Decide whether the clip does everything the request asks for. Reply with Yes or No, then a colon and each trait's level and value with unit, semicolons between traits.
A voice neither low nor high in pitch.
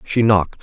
No: low, 100 Hz